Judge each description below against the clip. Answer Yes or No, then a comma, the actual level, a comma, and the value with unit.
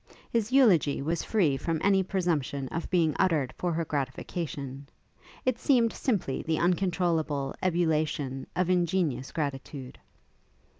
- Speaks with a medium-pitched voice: Yes, medium, 165 Hz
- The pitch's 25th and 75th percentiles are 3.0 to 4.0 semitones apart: No, average, 4.5 semitones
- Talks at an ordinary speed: No, slow, 120 wpm